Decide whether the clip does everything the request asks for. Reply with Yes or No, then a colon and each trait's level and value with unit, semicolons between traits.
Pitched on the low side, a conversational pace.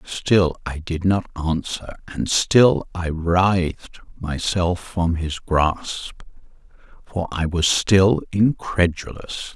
No: very low, 90 Hz; slow, 115 wpm